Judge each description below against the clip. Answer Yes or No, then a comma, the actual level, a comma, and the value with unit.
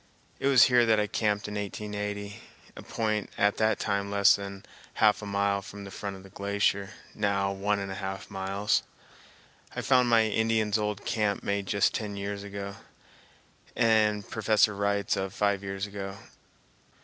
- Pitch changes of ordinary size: No, narrow, 1.1 semitones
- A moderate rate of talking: Yes, average, 170 wpm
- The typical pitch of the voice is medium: No, low, 100 Hz